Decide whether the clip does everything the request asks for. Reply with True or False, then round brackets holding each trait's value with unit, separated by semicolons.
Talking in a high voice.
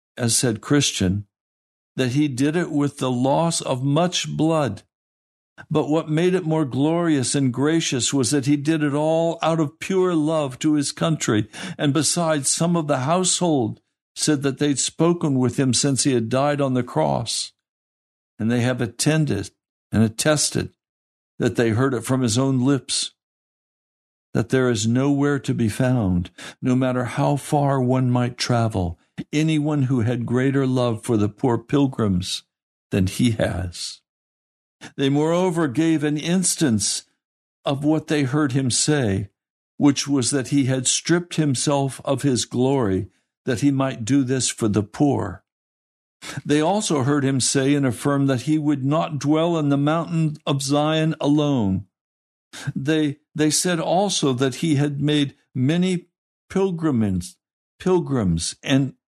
False (140 Hz)